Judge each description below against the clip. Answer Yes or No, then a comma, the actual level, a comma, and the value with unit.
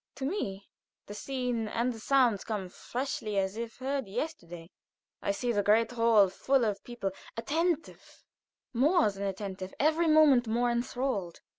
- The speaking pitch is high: Yes, high, 235 Hz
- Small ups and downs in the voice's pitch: No, average, 5.0 semitones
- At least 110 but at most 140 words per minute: No, average, 150 wpm